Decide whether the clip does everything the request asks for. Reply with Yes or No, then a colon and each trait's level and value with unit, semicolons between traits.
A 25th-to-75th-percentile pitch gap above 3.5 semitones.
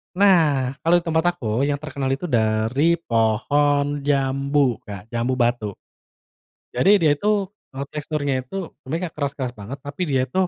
Yes: average, 4.2 semitones